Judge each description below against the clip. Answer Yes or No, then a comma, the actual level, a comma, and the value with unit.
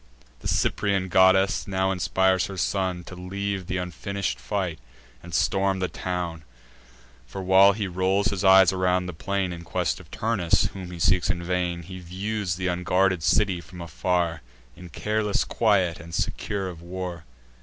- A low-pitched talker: Yes, very low, 95 Hz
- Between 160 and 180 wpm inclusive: Yes, average, 165 wpm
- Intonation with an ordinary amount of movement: No, narrow, 1.7 semitones